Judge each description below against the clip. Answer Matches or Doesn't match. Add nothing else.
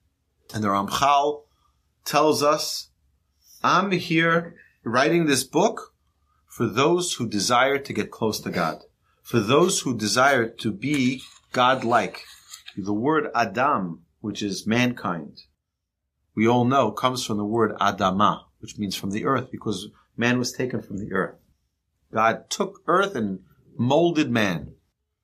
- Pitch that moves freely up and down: Matches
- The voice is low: Matches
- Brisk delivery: Doesn't match